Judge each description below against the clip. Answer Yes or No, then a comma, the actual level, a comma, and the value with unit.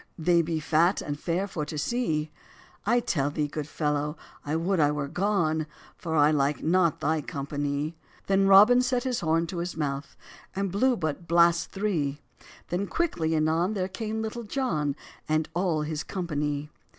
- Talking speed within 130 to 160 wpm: No, average, 170 wpm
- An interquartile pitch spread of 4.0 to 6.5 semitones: Yes, average, 4.4 semitones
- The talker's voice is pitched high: No, medium, 165 Hz